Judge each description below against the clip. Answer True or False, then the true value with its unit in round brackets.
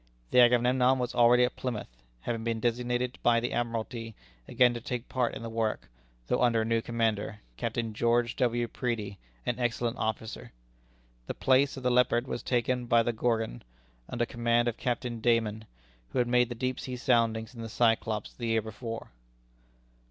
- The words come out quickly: False (175 wpm)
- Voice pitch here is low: True (120 Hz)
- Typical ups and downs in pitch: False (1.4 semitones)